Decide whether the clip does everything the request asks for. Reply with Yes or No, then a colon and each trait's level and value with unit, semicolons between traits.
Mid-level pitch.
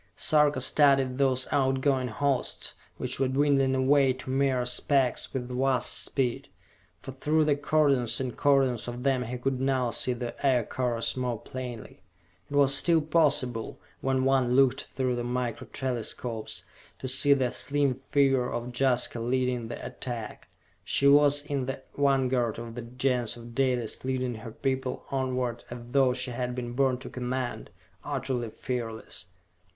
No: low, 130 Hz